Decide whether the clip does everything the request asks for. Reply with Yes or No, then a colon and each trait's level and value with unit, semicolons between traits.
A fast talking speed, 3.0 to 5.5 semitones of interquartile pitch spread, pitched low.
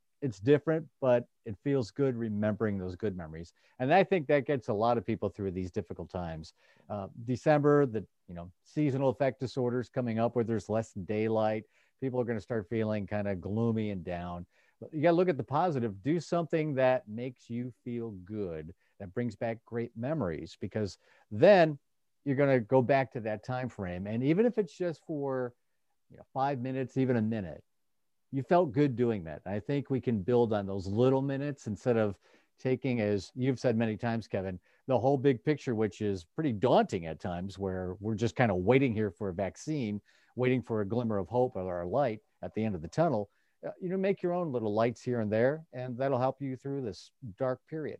Yes: fast, 210 wpm; average, 4.5 semitones; low, 120 Hz